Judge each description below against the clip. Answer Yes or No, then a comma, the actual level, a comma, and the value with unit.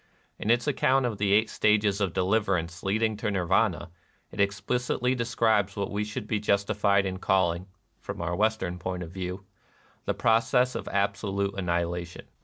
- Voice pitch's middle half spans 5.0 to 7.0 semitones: No, average, 2.9 semitones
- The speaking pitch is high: No, low, 100 Hz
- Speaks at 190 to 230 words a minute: No, average, 170 wpm